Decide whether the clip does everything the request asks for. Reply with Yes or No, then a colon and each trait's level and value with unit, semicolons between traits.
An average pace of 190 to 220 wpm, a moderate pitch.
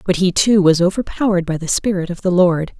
No: fast, 235 wpm; medium, 180 Hz